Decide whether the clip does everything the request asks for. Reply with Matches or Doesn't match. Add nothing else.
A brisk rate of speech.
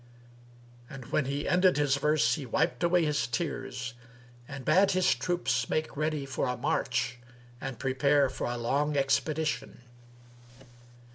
Doesn't match